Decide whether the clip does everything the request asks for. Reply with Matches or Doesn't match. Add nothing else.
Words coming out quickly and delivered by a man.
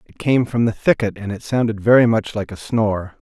Matches